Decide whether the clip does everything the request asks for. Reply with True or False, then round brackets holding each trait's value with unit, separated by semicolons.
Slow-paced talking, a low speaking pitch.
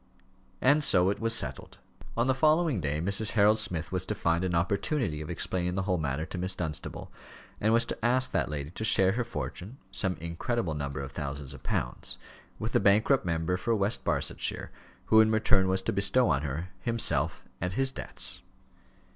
False (190 wpm; 95 Hz)